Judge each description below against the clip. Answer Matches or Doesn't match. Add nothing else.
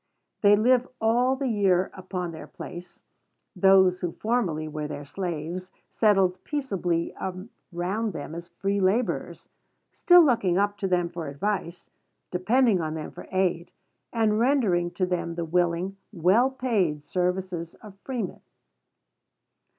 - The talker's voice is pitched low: Doesn't match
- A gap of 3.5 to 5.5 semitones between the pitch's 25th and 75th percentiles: Matches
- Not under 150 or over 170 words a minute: Doesn't match